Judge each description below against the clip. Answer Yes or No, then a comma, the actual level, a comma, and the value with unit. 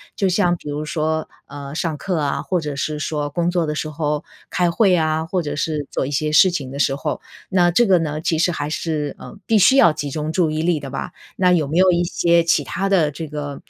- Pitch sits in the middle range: Yes, medium, 155 Hz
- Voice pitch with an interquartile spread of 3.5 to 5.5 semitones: No, average, 2.8 semitones